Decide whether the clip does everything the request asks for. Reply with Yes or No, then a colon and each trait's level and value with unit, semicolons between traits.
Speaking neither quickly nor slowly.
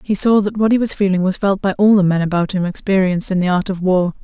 No: fast, 300 wpm